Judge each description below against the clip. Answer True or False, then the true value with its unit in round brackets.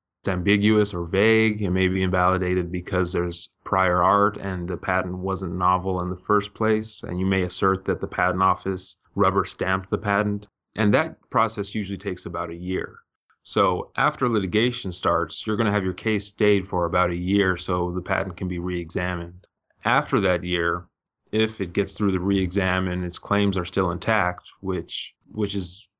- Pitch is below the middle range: True (95 Hz)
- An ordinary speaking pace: True (185 wpm)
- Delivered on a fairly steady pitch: True (2.3 semitones)